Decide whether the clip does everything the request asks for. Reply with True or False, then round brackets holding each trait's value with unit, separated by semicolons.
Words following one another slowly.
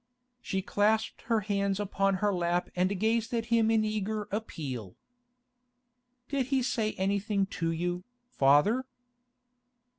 True (125 wpm)